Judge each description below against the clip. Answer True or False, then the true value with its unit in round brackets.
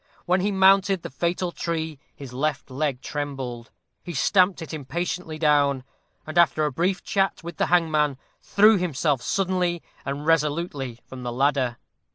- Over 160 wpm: False (155 wpm)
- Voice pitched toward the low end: False (155 Hz)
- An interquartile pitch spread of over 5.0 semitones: False (4.3 semitones)